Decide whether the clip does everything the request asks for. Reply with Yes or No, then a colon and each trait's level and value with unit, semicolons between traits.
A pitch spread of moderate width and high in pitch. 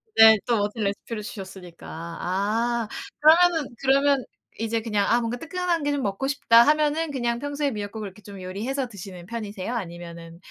No: wide, 5.7 semitones; high, 230 Hz